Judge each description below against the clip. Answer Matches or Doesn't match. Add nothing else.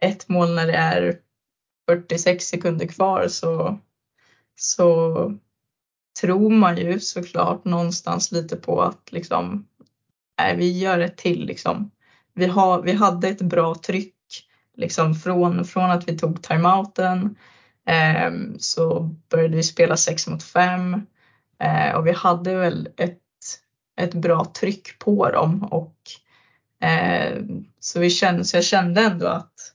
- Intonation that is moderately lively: Doesn't match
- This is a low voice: Doesn't match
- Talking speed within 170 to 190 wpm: Doesn't match